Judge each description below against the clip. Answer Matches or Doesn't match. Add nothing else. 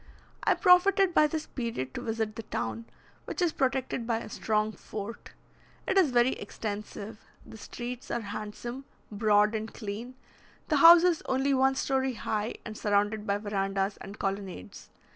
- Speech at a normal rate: Matches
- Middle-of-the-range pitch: Doesn't match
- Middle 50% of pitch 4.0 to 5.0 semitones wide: Matches